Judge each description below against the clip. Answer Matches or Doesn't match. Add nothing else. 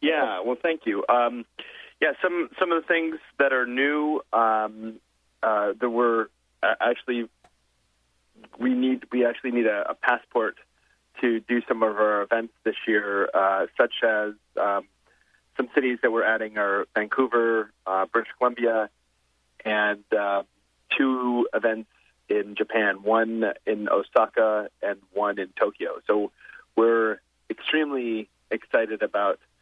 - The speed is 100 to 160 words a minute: Matches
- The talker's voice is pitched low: Matches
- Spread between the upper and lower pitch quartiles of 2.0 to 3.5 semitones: Matches